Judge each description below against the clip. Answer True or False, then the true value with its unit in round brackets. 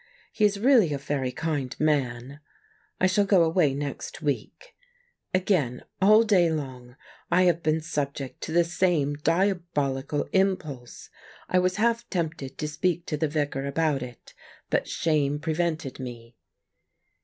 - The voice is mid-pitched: True (155 Hz)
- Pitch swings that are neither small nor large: True (4.6 semitones)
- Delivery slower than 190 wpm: True (145 wpm)